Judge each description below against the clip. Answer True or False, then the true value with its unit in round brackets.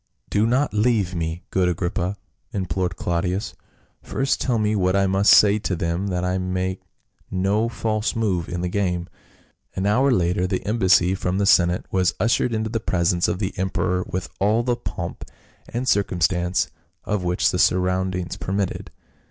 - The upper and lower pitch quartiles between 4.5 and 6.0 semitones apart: False (2.7 semitones)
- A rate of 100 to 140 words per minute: False (175 wpm)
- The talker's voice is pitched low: True (95 Hz)